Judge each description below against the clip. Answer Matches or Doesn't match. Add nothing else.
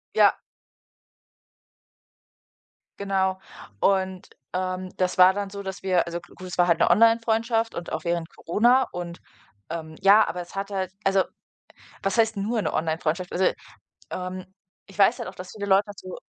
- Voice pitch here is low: Doesn't match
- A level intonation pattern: Matches